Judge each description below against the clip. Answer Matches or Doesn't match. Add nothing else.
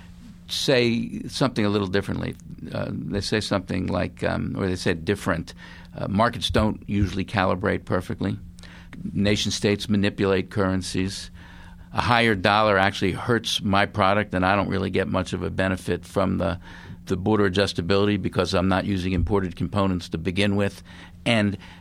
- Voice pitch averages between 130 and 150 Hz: Doesn't match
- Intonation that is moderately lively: Doesn't match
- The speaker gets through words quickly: Doesn't match